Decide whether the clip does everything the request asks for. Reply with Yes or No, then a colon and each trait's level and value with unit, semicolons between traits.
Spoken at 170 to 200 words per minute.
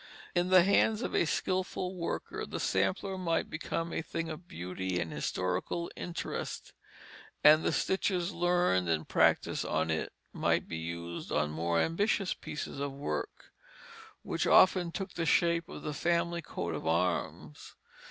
No: average, 150 wpm